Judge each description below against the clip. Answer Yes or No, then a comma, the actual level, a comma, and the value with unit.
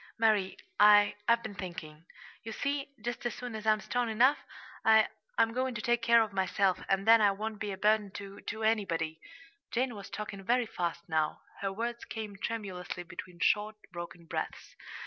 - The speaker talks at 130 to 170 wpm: No, average, 185 wpm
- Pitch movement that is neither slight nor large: Yes, average, 3.0 semitones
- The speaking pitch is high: Yes, high, 210 Hz